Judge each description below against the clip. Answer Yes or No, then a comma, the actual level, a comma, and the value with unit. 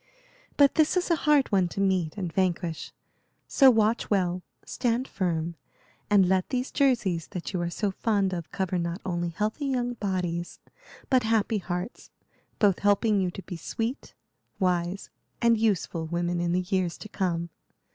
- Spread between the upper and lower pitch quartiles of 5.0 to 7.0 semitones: No, average, 4.5 semitones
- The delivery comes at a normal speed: Yes, average, 165 wpm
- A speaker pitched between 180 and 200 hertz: Yes, high, 190 Hz